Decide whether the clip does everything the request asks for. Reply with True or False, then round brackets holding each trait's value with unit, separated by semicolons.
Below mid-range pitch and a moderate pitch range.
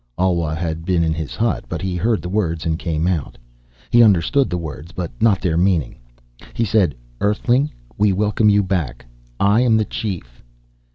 True (90 Hz; 4.4 semitones)